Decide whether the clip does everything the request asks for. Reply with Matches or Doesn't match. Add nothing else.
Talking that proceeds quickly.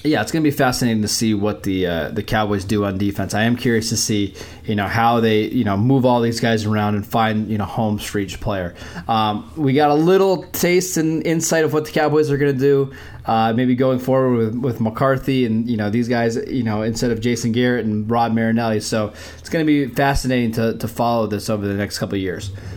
Matches